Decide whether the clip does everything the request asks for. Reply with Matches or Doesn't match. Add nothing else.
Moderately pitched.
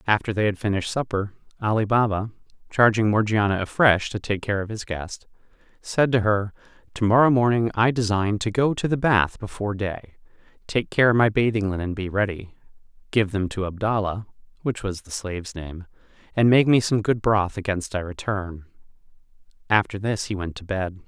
Doesn't match